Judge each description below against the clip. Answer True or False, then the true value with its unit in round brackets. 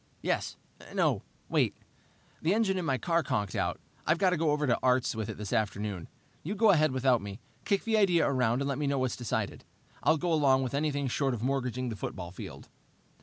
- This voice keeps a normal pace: False (215 wpm)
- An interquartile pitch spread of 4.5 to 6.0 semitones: True (5.0 semitones)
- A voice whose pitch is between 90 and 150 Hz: True (135 Hz)